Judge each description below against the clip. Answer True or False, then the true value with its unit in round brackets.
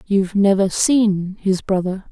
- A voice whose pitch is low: False (195 Hz)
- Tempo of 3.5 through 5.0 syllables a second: True (4.1 syllables/s)